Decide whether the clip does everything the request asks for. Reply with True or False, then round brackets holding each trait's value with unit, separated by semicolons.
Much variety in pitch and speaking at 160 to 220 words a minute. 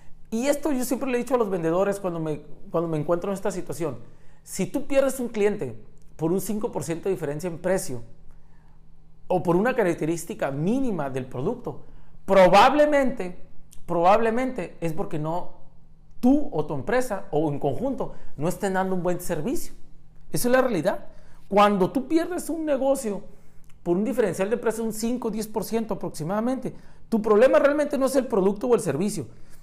True (6.5 semitones; 170 wpm)